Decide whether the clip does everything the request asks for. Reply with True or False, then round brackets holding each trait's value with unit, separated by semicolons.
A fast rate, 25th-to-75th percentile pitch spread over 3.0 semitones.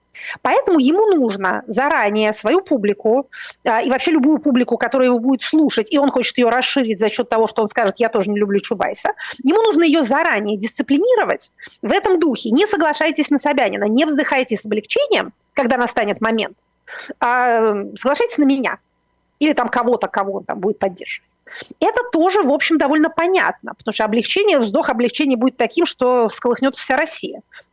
True (170 wpm; 5.5 semitones)